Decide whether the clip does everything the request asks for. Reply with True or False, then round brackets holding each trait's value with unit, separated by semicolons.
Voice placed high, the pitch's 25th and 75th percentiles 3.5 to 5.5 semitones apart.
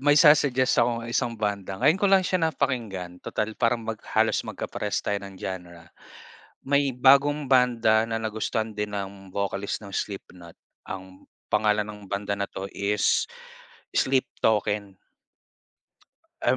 False (110 Hz; 4.3 semitones)